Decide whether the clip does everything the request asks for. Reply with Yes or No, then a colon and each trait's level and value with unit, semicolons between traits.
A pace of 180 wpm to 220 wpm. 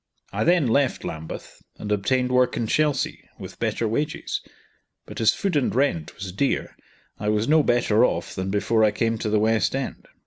Yes: average, 185 wpm